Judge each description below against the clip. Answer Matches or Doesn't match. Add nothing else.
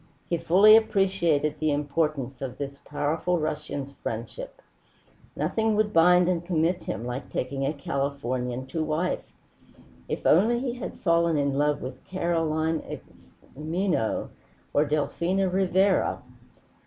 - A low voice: Doesn't match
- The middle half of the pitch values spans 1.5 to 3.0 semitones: Doesn't match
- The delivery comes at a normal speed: Doesn't match